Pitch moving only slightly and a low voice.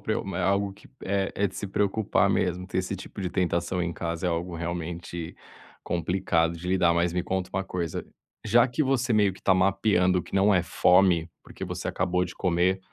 Yes: narrow, 2.0 semitones; very low, 90 Hz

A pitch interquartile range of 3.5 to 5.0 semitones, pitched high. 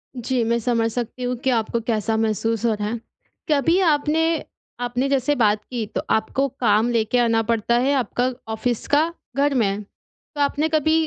Yes: average, 3.9 semitones; high, 240 Hz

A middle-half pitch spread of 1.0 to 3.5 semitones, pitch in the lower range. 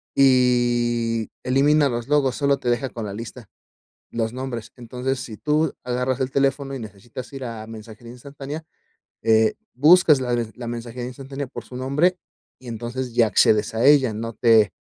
Yes: average, 2.8 semitones; low, 125 Hz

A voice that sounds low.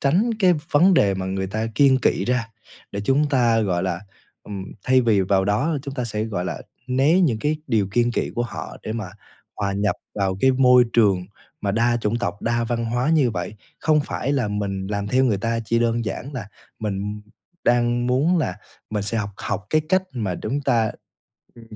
Yes: low, 115 Hz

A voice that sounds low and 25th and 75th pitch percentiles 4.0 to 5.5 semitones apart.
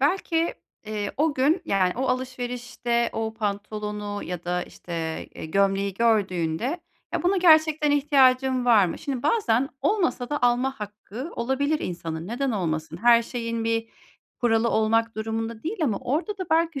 No: high, 235 Hz; average, 5.1 semitones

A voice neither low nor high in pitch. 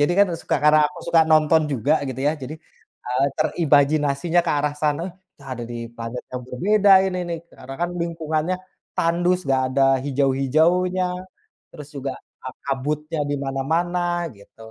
Yes: medium, 150 Hz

